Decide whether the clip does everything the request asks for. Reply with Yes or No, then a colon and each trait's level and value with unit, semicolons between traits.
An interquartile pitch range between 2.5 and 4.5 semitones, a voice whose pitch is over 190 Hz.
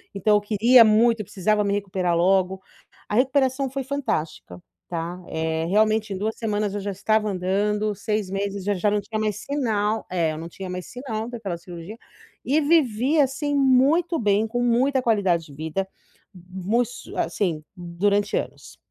Yes: average, 4.2 semitones; high, 210 Hz